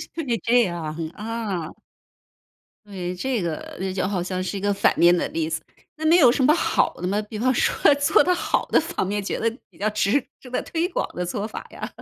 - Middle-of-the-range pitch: No, high, 205 Hz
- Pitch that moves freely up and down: Yes, wide, 5.8 semitones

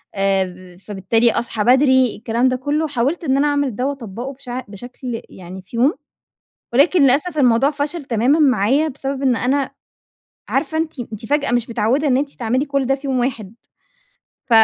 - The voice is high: Yes, very high, 255 Hz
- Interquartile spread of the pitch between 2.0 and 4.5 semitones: Yes, average, 3.7 semitones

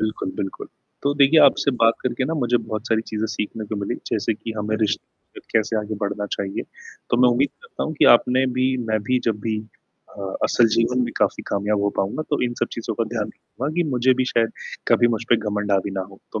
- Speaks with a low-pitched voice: Yes, low, 115 Hz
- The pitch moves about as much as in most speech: Yes, average, 3.3 semitones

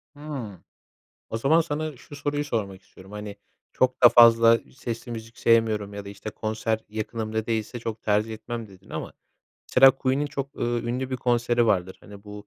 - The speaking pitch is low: Yes, low, 115 Hz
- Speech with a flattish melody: No, average, 3.2 semitones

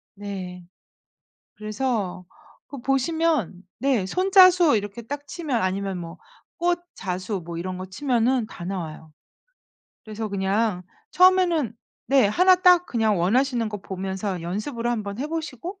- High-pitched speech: Yes, high, 220 Hz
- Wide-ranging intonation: Yes, wide, 7.1 semitones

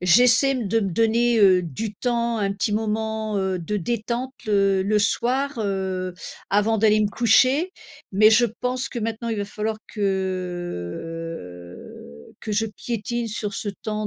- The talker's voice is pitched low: No, high, 215 Hz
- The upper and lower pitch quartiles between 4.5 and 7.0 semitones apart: No, average, 3.3 semitones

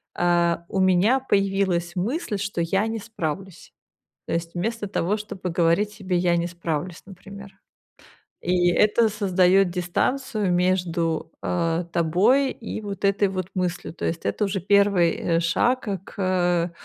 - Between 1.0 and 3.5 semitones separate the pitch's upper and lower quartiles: Yes, average, 2.8 semitones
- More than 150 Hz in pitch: Yes, medium, 185 Hz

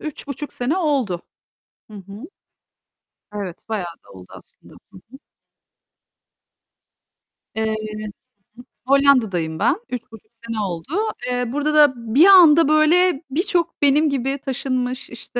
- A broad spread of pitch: Yes, wide, 5.7 semitones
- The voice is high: Yes, very high, 255 Hz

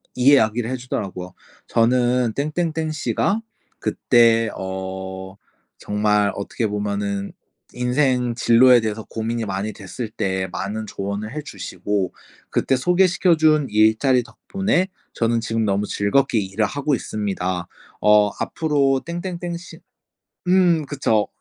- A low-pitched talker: Yes, low, 115 Hz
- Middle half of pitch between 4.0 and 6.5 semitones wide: Yes, average, 5.2 semitones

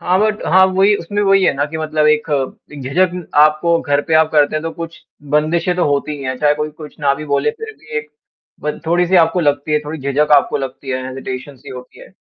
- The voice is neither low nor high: Yes, medium, 150 Hz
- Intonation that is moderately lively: Yes, average, 3.0 semitones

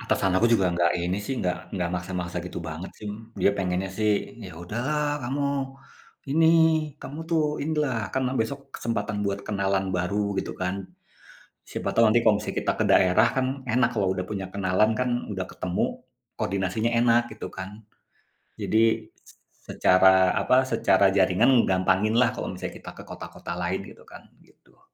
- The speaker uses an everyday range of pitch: Yes, average, 4.0 semitones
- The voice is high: No, low, 100 Hz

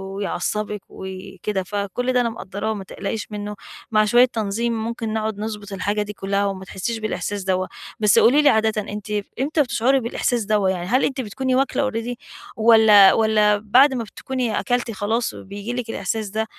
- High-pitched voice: Yes, high, 215 Hz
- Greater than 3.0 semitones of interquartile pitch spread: No, average, 2.7 semitones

